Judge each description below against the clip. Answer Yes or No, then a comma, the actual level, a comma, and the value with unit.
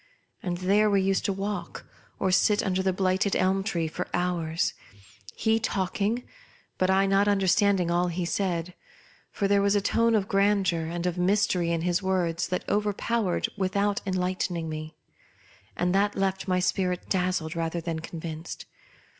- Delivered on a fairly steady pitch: Yes, narrow, 2.3 semitones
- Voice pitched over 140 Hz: Yes, medium, 185 Hz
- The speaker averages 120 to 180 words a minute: Yes, average, 170 wpm